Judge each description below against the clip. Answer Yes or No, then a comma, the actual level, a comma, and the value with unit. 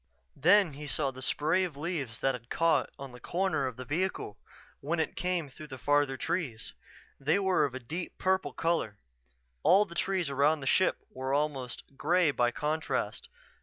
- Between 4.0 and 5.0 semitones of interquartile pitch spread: Yes, average, 4.4 semitones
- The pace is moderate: Yes, average, 180 wpm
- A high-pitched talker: No, medium, 150 Hz